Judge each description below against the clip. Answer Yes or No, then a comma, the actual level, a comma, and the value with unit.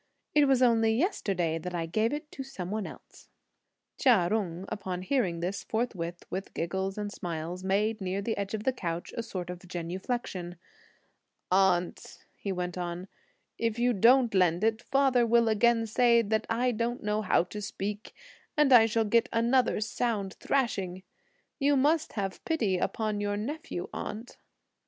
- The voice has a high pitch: Yes, high, 210 Hz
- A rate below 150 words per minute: No, average, 160 wpm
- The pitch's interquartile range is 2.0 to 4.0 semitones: No, average, 4.4 semitones